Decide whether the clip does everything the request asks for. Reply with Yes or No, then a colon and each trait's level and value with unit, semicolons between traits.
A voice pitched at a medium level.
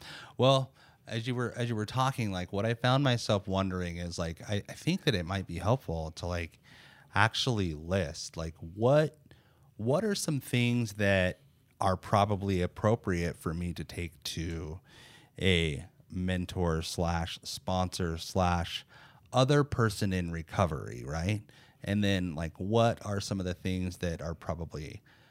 No: low, 100 Hz